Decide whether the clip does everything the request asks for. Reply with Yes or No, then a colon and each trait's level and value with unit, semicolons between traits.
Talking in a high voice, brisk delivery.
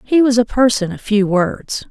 Yes: high, 225 Hz; fast, 220 wpm